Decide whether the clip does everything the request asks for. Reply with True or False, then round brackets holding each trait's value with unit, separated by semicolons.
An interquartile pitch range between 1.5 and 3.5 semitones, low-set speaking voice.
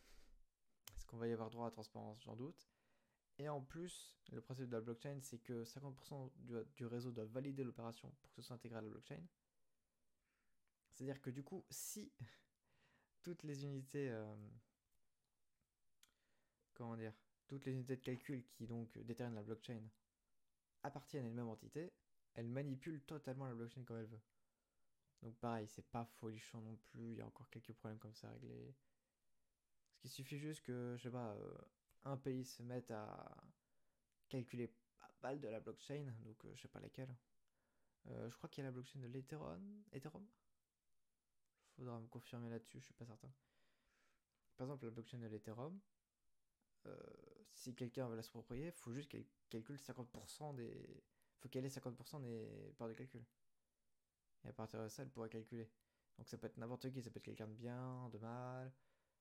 True (3.0 semitones; 120 Hz)